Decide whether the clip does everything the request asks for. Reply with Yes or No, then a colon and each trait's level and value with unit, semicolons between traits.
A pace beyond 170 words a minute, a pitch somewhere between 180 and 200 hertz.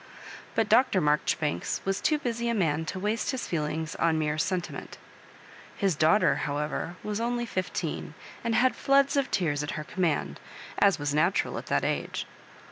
Yes: average, 180 wpm; medium, 185 Hz